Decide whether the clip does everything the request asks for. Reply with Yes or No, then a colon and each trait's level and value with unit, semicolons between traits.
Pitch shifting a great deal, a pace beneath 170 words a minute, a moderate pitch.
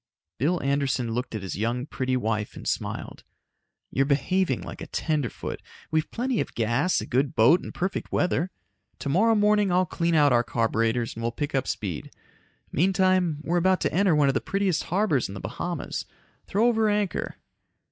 No: wide, 7.2 semitones; average, 180 wpm; medium, 150 Hz